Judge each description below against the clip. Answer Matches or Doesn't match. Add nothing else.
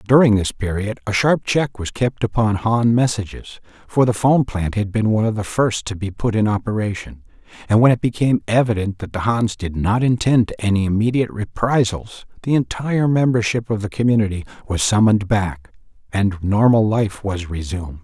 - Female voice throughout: Doesn't match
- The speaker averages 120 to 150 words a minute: Doesn't match